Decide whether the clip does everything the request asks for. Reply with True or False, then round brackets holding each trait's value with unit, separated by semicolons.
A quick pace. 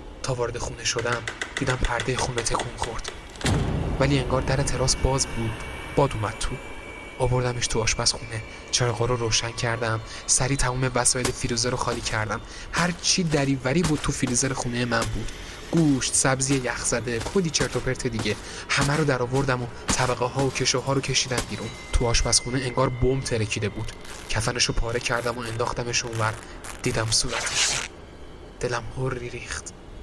True (160 wpm)